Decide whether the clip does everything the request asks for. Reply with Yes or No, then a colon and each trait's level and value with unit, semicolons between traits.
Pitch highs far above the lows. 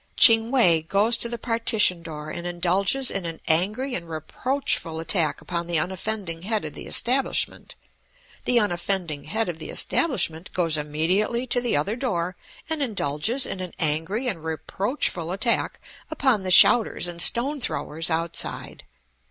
Yes: wide, 6.0 semitones